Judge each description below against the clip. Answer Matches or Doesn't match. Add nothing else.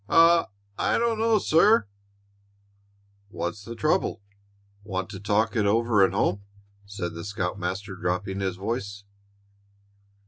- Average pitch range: Matches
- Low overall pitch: Matches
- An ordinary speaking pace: Doesn't match